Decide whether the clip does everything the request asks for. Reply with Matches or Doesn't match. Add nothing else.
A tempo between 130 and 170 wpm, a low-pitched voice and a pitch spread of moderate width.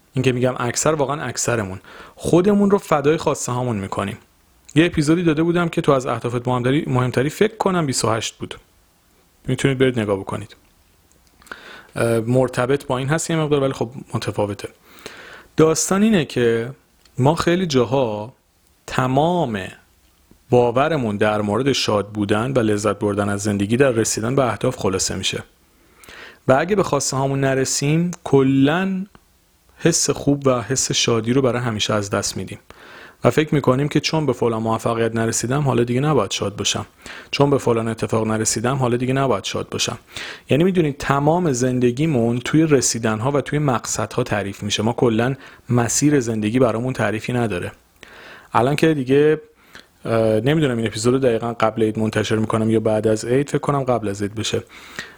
Matches